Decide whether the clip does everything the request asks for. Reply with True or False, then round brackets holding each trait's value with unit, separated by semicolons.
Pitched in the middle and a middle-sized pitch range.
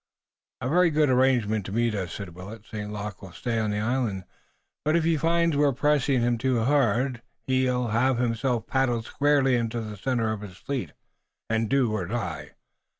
False (120 Hz; 3.8 semitones)